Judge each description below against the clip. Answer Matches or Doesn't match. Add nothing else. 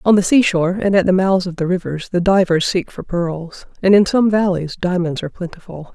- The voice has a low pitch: Doesn't match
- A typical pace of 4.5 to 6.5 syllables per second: Matches